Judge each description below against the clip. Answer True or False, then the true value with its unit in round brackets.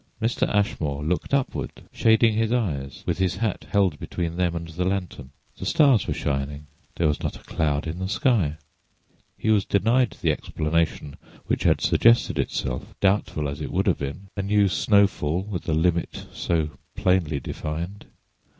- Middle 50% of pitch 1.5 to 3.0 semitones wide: False (5.1 semitones)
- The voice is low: True (90 Hz)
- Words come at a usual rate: True (165 wpm)